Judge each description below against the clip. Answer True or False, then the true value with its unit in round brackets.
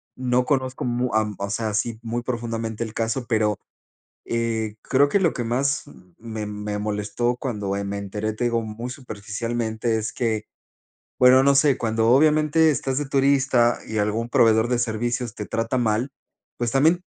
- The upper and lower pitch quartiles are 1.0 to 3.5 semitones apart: True (2.9 semitones)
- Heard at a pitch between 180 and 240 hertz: False (115 Hz)